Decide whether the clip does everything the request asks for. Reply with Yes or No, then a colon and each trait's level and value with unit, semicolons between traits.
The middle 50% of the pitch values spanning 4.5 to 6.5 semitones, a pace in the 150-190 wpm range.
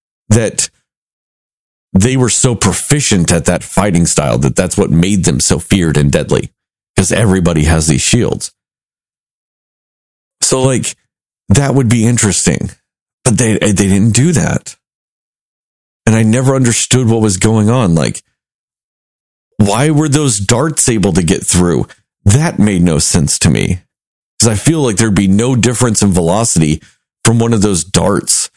Yes: average, 5.1 semitones; average, 155 wpm